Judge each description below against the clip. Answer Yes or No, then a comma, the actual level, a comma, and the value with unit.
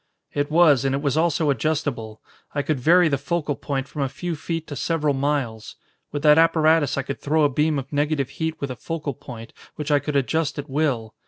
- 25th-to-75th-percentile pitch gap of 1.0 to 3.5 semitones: Yes, narrow, 2.5 semitones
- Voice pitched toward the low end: No, medium, 145 Hz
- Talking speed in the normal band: No, fast, 220 wpm